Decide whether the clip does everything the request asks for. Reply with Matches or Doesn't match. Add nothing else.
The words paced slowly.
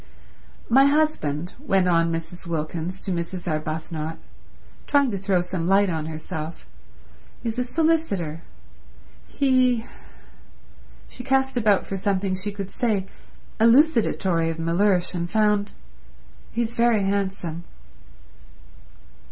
Matches